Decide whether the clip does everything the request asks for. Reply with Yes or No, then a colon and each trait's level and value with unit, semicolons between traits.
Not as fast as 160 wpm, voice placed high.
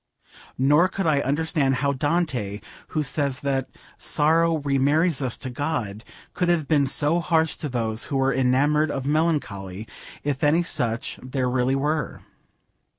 No: average, 150 wpm; medium, 140 Hz